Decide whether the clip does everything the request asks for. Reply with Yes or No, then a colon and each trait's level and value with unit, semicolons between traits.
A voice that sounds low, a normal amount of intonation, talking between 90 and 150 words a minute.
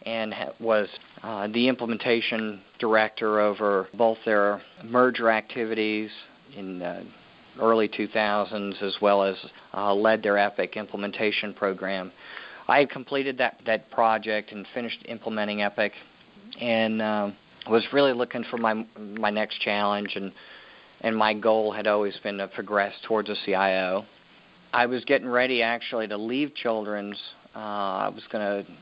No: low, 110 Hz; narrow, 2.0 semitones; average, 145 wpm